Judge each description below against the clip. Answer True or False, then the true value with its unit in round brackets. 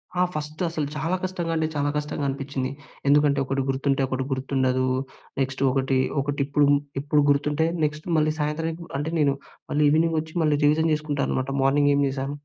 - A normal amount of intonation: False (2.1 semitones)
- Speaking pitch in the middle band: True (145 Hz)